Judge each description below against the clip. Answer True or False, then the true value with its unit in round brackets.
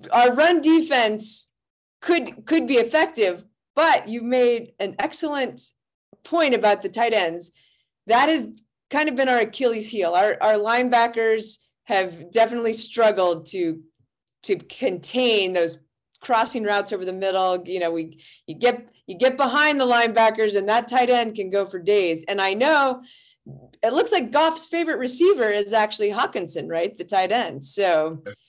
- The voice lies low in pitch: False (225 Hz)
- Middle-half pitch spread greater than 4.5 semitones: True (5.1 semitones)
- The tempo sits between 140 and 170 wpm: True (160 wpm)